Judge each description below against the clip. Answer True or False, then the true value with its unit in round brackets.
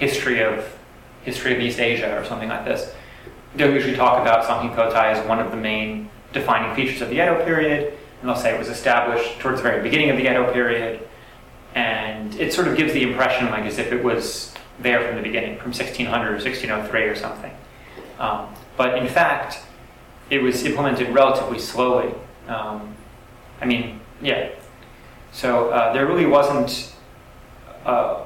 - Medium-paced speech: True (170 wpm)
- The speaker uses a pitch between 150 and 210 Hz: False (120 Hz)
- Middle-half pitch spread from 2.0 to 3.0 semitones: True (2.7 semitones)